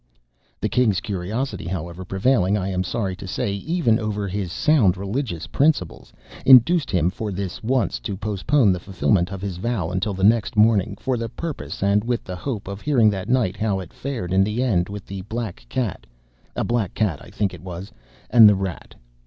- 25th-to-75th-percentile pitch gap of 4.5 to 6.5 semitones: No, average, 4.0 semitones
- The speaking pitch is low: Yes, low, 100 Hz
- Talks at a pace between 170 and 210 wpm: Yes, average, 195 wpm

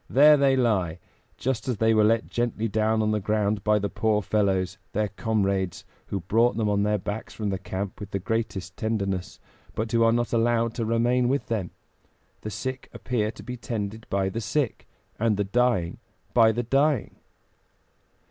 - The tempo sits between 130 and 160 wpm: No, average, 185 wpm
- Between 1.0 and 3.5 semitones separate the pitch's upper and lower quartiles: Yes, narrow, 2.6 semitones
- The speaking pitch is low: Yes, low, 110 Hz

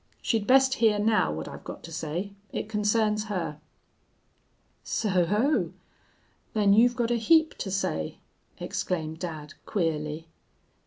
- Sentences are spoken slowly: Yes, slow, 130 wpm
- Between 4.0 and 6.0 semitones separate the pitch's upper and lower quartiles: Yes, wide, 5.6 semitones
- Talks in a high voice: Yes, high, 205 Hz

